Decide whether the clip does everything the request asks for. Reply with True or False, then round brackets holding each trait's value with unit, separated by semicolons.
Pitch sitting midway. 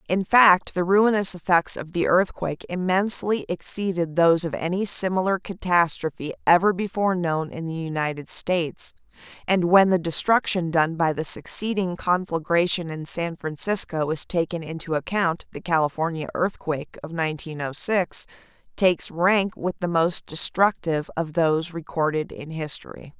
True (170 Hz)